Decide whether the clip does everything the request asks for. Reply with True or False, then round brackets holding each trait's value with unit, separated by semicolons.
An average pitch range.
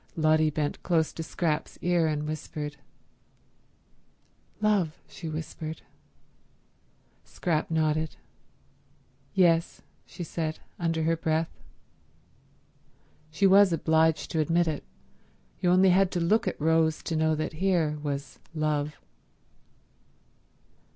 False (1.9 semitones)